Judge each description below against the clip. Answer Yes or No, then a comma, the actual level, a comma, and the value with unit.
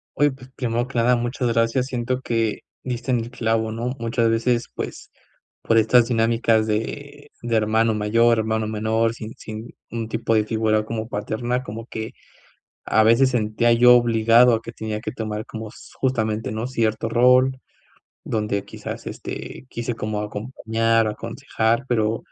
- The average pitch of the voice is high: No, low, 115 Hz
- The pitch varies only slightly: Yes, narrow, 1.6 semitones